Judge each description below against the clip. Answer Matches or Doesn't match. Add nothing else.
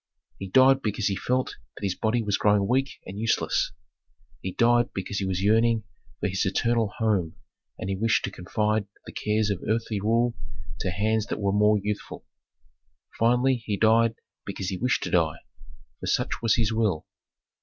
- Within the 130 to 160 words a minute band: Doesn't match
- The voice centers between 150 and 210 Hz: Doesn't match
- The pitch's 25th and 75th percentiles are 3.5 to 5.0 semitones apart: Doesn't match